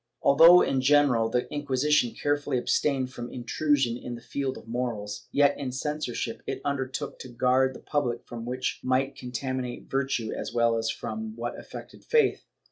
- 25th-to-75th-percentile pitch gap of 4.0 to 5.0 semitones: No, average, 2.9 semitones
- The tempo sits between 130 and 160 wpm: No, average, 170 wpm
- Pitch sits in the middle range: No, low, 130 Hz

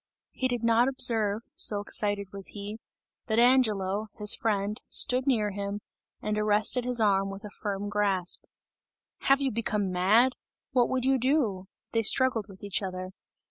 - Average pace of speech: Yes, average, 160 wpm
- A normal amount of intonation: Yes, average, 3.3 semitones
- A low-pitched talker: No, high, 210 Hz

